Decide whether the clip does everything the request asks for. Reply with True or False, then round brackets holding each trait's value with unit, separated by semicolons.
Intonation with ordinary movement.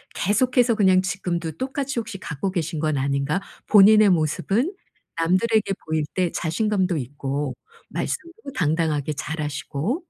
False (6.0 semitones)